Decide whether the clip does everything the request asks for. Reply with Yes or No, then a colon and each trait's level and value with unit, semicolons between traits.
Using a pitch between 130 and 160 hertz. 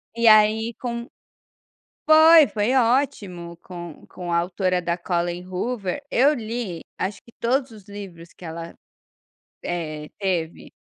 No: high, 195 Hz